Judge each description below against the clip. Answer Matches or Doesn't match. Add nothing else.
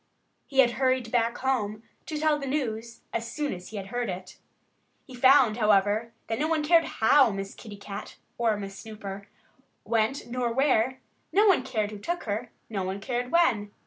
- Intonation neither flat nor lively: Matches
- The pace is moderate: Matches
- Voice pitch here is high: Matches